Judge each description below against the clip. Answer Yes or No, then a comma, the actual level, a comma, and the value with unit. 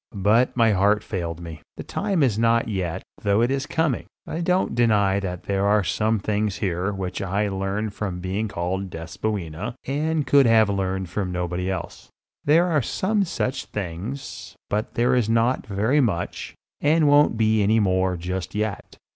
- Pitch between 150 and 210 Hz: No, low, 105 Hz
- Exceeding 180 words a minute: No, average, 175 wpm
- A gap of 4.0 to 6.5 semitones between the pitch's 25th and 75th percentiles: Yes, average, 4.3 semitones